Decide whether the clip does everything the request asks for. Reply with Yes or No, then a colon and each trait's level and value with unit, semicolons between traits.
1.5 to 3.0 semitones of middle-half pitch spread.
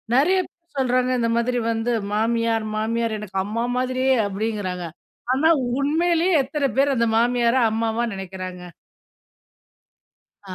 No: average, 3.5 semitones